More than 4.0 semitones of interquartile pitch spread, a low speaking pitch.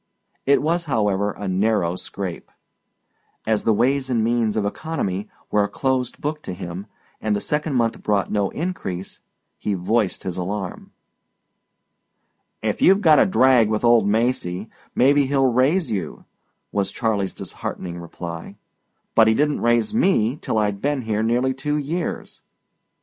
Yes: average, 5.3 semitones; low, 110 Hz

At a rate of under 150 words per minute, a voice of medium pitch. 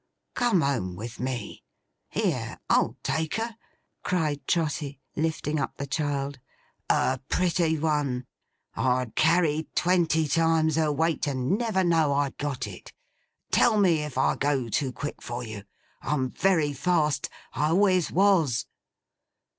Yes: slow, 135 wpm; medium, 150 Hz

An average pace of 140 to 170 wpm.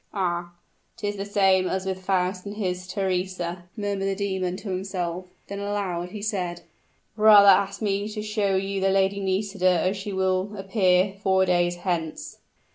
Yes: average, 165 wpm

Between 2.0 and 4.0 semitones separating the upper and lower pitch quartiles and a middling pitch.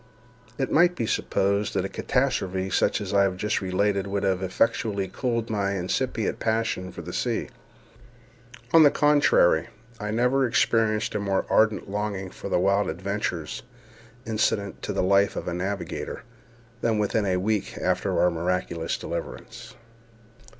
No: average, 2.8 semitones; low, 100 Hz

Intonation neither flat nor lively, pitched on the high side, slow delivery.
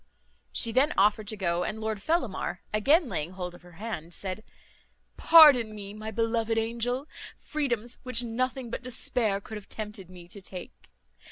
No: average, 3.7 semitones; high, 220 Hz; average, 165 wpm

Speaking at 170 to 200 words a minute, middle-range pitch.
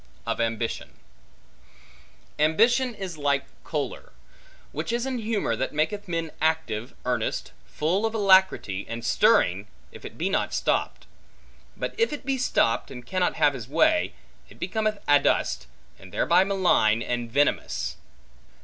No: average, 140 wpm; medium, 160 Hz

